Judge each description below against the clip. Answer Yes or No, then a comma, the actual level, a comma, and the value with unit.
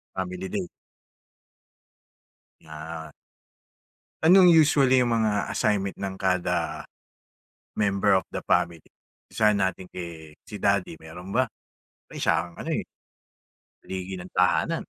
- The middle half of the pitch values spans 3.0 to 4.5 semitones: Yes, average, 3.3 semitones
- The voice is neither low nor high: No, very low, 95 Hz